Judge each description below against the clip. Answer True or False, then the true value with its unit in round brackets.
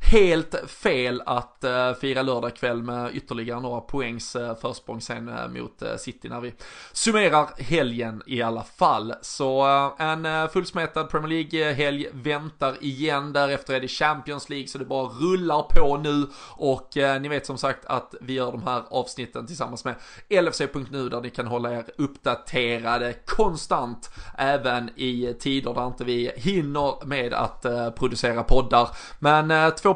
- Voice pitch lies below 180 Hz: True (135 Hz)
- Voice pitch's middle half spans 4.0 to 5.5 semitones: False (3.3 semitones)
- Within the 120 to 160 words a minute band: True (145 wpm)